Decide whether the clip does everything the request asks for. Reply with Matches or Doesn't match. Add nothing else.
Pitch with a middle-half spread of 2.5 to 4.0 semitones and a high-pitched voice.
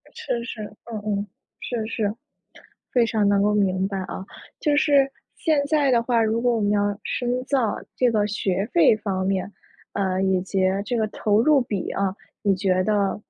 Matches